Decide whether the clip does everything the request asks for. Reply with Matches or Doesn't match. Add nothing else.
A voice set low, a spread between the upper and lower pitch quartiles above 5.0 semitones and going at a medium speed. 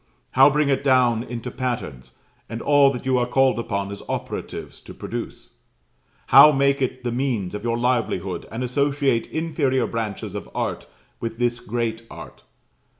Doesn't match